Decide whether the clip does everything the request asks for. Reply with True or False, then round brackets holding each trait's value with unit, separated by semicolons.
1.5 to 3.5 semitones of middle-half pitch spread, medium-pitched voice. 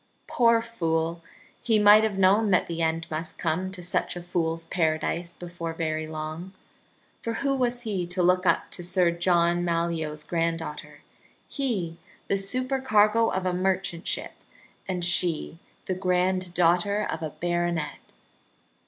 True (2.8 semitones; 175 Hz)